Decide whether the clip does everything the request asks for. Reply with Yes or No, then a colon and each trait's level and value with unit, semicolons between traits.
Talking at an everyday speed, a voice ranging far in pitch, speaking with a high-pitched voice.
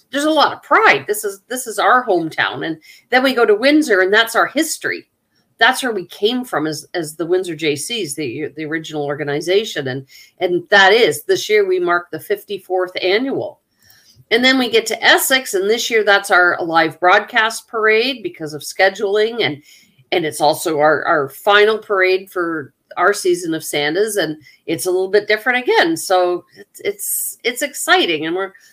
Yes: average, 190 wpm; wide, 7.3 semitones; high, 200 Hz